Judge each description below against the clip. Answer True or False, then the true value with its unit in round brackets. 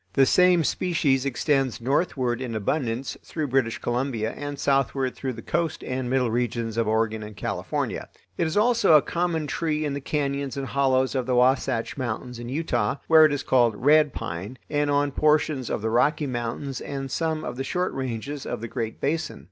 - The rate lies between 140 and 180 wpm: False (190 wpm)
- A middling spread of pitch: True (3.8 semitones)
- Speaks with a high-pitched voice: False (135 Hz)